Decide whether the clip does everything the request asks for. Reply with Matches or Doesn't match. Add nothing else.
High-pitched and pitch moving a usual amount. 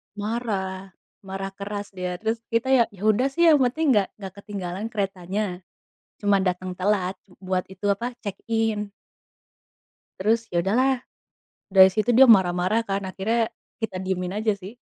Matches